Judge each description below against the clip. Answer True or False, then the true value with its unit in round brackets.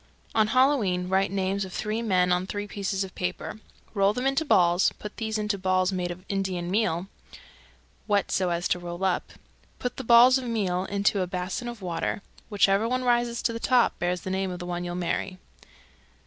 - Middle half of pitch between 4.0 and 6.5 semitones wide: False (3.5 semitones)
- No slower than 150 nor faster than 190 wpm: False (200 wpm)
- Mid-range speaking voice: False (195 Hz)